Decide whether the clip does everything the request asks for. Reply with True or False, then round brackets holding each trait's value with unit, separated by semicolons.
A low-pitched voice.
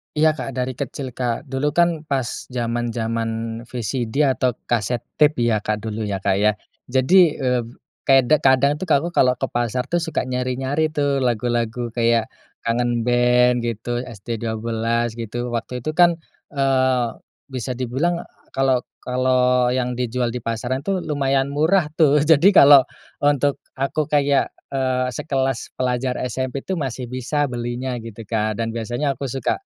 True (125 Hz)